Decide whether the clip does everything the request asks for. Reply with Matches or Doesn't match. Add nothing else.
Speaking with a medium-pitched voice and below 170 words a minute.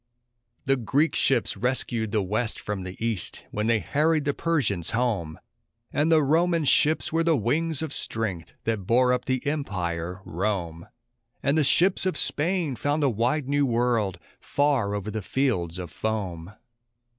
Doesn't match